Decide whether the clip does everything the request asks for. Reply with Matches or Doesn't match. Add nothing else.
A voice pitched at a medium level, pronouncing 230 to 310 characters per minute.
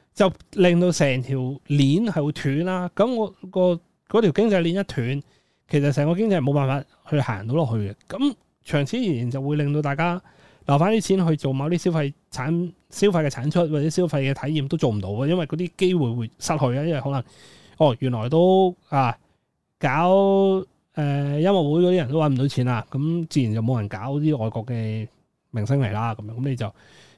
Matches